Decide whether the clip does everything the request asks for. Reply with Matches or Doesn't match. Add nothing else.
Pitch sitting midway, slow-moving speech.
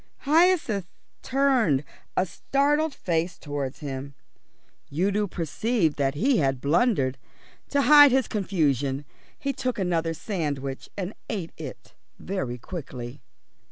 Matches